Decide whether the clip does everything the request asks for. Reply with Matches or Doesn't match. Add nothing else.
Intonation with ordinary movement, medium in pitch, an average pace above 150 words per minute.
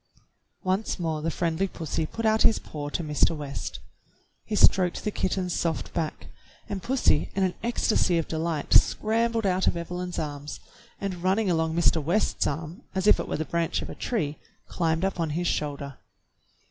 Matches